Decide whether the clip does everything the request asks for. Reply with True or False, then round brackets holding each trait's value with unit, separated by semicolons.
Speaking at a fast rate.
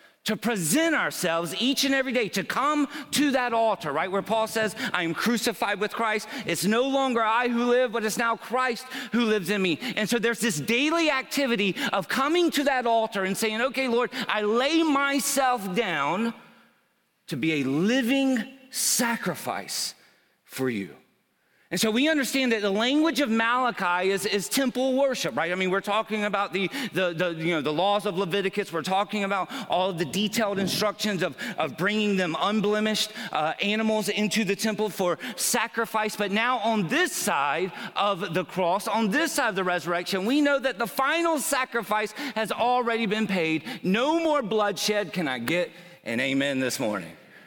False (180 wpm)